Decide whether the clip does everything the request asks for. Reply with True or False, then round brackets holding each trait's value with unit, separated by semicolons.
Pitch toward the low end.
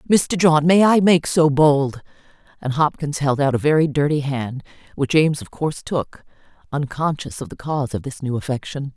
False (150 Hz)